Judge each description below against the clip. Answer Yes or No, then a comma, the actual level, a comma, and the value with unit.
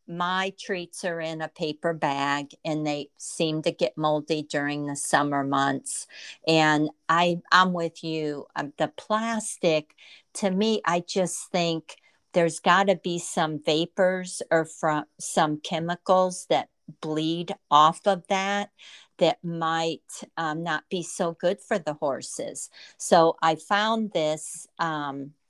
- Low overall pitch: No, medium, 165 Hz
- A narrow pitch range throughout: No, average, 3.0 semitones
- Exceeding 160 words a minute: No, slow, 135 wpm